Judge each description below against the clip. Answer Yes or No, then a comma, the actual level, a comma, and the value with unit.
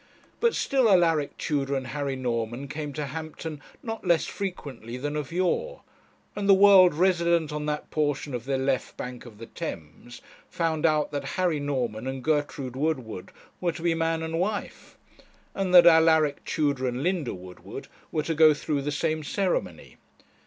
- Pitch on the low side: No, medium, 150 Hz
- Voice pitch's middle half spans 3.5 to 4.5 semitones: Yes, average, 4.1 semitones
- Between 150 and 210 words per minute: Yes, average, 170 wpm